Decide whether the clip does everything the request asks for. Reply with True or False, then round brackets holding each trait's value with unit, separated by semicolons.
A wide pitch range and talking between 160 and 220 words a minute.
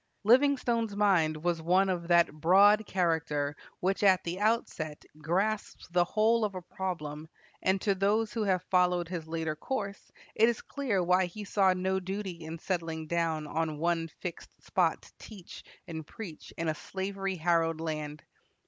False (3.5 semitones; 165 wpm)